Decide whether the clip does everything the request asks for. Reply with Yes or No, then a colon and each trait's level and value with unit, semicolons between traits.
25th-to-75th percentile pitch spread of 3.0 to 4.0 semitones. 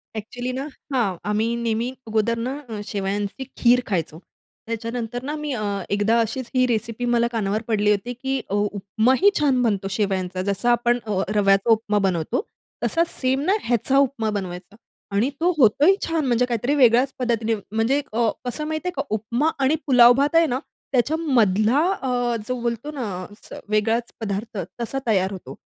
Yes: average, 3.6 semitones